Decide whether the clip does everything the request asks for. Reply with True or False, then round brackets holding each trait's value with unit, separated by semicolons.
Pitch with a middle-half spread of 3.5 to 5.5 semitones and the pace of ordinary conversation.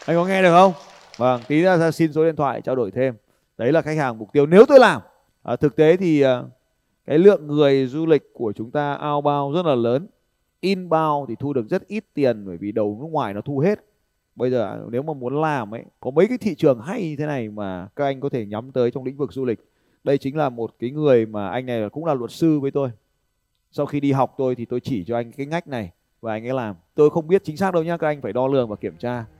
False (4.7 semitones; 270 wpm)